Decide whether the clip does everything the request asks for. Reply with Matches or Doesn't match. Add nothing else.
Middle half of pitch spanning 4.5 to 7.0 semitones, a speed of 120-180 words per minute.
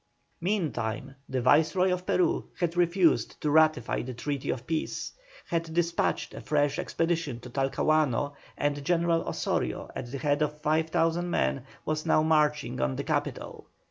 Doesn't match